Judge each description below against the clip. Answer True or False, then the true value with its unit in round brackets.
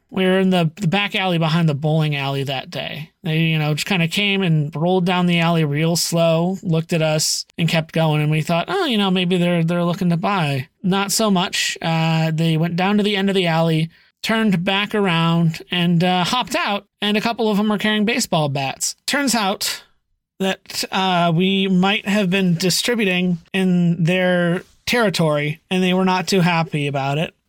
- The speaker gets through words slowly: False (205 wpm)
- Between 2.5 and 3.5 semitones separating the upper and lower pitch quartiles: True (3.1 semitones)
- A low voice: False (180 Hz)